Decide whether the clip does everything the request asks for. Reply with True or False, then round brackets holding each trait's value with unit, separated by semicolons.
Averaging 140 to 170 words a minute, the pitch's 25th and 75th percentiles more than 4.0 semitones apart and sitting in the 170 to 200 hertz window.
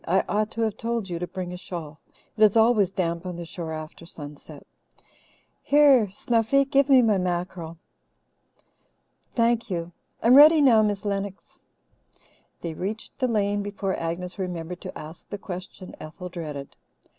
True (155 wpm; 4.5 semitones; 190 Hz)